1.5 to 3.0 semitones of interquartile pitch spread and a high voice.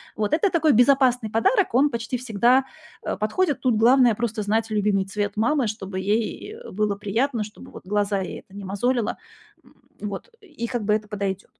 No: average, 3.9 semitones; high, 220 Hz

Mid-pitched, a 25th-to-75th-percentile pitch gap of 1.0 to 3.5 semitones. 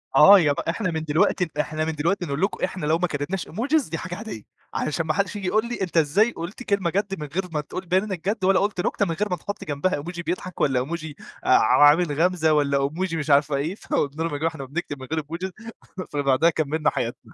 No: medium, 165 Hz; average, 4.0 semitones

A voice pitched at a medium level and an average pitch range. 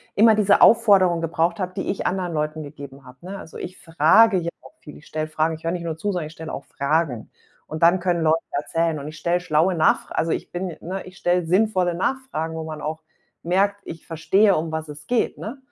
Yes: medium, 165 Hz; average, 3.1 semitones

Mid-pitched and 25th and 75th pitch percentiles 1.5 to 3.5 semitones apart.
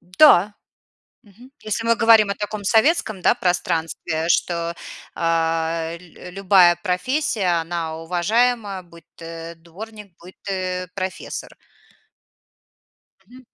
No: medium, 180 Hz; average, 4.2 semitones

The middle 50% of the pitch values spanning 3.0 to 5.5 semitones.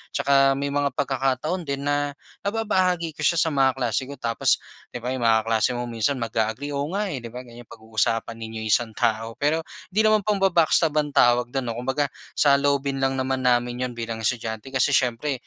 Yes: average, 3.6 semitones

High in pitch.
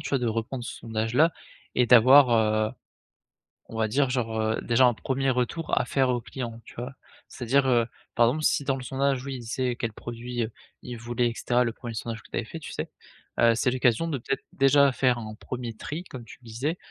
No: low, 125 Hz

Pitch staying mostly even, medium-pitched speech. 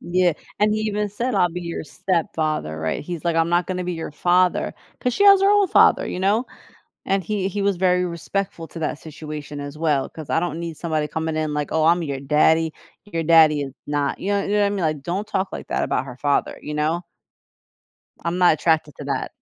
No: average, 3.7 semitones; medium, 170 Hz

